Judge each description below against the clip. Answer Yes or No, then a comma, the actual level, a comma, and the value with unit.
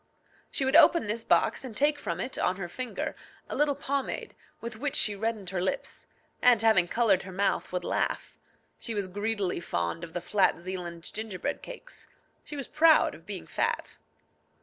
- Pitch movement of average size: No, wide, 6.1 semitones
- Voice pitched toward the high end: Yes, high, 215 Hz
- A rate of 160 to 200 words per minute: Yes, average, 180 wpm